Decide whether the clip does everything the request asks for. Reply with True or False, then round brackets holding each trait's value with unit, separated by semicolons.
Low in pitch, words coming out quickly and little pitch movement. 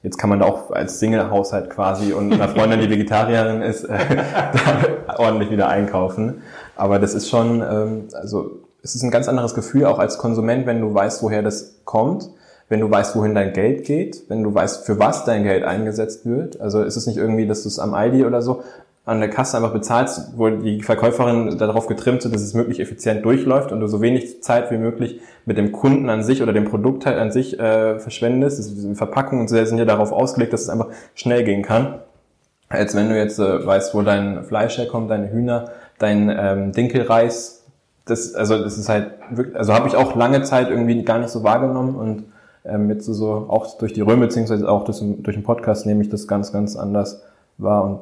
True (110 Hz; 220 wpm; 2.0 semitones)